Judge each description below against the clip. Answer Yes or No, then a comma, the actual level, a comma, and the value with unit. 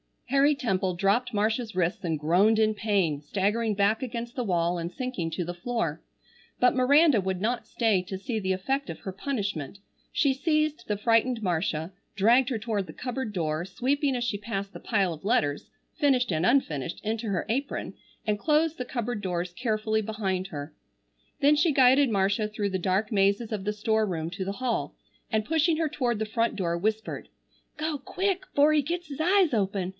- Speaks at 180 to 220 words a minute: Yes, average, 190 wpm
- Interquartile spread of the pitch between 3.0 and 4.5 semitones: No, average, 5.1 semitones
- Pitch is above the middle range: Yes, high, 215 Hz